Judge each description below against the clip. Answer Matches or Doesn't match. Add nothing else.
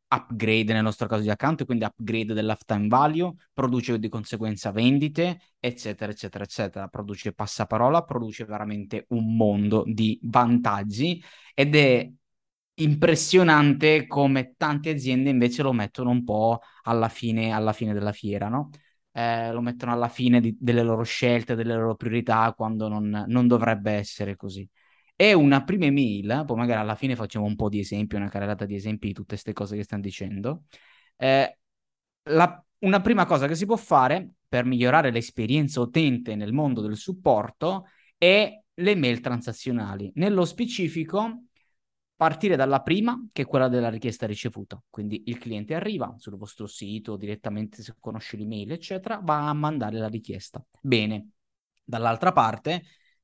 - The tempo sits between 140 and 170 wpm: Matches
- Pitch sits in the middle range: Doesn't match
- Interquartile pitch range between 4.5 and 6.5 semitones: Matches